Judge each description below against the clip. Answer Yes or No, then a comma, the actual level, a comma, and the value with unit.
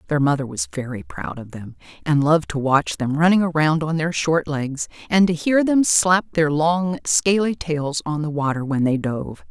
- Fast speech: Yes, fast, 210 wpm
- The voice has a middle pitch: Yes, medium, 150 Hz